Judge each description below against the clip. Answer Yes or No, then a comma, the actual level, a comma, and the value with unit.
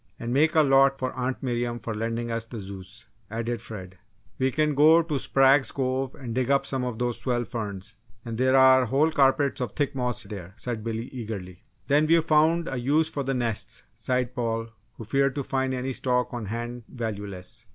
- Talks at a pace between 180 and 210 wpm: Yes, average, 200 wpm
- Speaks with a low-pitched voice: Yes, low, 125 Hz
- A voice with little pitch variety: No, average, 3.0 semitones